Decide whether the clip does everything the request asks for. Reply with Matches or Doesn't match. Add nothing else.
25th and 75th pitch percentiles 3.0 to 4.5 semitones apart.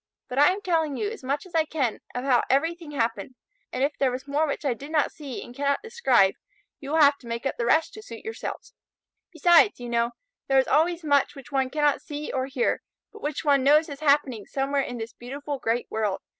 Matches